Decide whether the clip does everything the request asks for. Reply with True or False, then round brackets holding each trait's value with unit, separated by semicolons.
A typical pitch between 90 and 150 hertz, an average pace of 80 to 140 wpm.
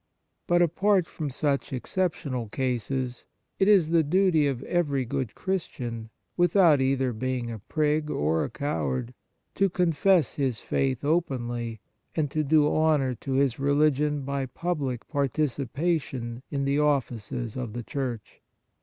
True (140 Hz; 135 wpm)